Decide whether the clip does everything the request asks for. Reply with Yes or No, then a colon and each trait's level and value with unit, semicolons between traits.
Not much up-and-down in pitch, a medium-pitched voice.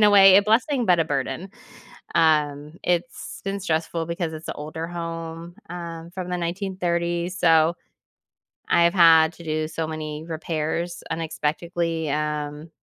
Yes: narrow, 1.7 semitones; medium, 165 Hz